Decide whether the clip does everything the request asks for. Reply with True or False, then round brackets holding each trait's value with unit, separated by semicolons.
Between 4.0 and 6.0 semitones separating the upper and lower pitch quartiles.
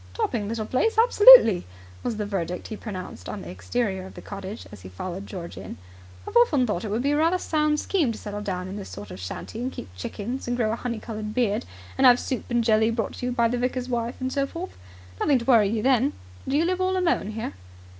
True (4.6 semitones)